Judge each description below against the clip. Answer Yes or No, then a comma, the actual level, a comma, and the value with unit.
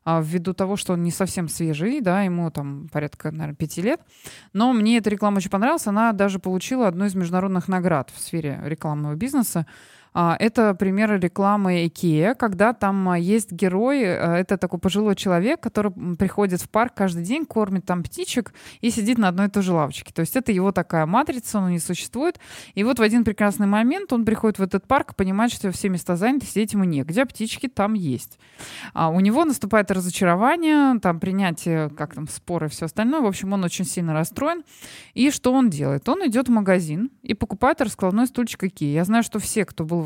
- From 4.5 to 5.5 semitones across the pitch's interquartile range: Yes, average, 4.8 semitones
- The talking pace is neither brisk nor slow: No, fast, 195 wpm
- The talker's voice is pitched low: No, high, 195 Hz